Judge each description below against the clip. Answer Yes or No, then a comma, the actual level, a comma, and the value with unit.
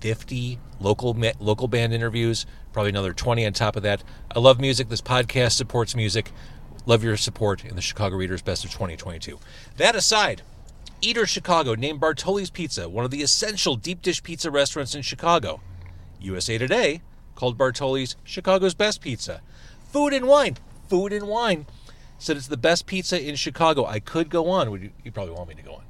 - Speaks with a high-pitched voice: No, low, 125 Hz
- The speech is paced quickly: No, average, 185 wpm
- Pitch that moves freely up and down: Yes, wide, 7.5 semitones